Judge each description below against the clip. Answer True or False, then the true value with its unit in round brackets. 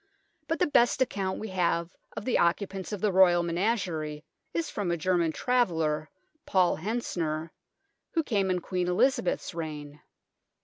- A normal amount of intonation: True (3.8 semitones)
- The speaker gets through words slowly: False (160 wpm)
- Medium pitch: True (180 Hz)